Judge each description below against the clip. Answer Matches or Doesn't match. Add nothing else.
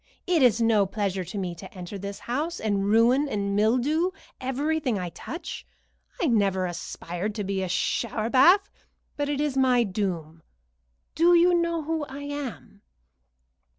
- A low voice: Doesn't match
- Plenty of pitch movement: Matches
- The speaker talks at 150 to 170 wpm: Matches